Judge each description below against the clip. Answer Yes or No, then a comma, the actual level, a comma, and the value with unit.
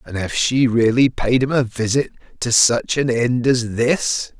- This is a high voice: No, low, 120 Hz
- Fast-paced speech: No, average, 190 wpm